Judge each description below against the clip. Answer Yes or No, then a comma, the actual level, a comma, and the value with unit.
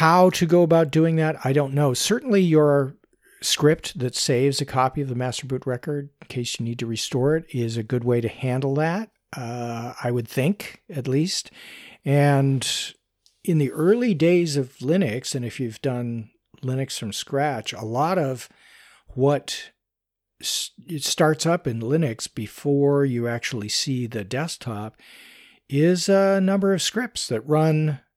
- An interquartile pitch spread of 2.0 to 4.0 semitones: No, average, 4.7 semitones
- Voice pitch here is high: No, medium, 140 Hz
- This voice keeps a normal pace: Yes, average, 165 wpm